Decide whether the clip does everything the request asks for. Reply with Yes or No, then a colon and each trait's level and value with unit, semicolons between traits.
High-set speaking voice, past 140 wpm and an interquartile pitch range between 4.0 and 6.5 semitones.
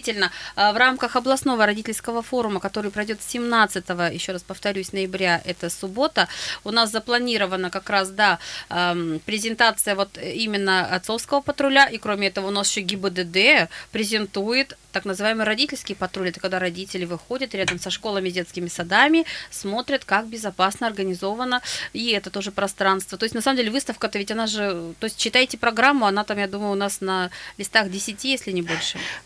No: high, 205 Hz; fast, 160 wpm; average, 3.3 semitones